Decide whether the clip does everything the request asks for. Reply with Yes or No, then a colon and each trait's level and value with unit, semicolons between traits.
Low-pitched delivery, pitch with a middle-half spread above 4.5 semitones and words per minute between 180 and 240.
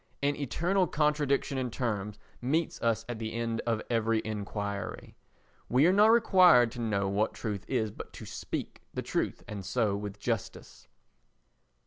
No: low, 115 Hz; average, 5.1 semitones; average, 155 wpm